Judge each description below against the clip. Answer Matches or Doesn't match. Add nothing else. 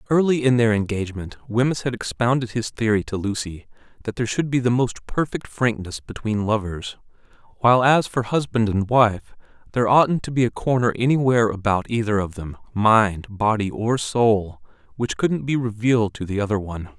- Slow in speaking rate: Doesn't match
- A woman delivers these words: Doesn't match